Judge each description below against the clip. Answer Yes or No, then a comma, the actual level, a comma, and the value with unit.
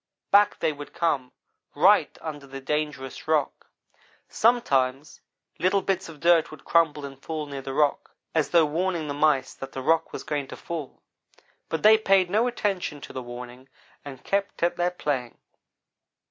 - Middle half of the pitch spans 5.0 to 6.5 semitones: No, average, 4.3 semitones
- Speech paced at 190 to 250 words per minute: No, average, 170 wpm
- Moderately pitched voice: Yes, medium, 150 Hz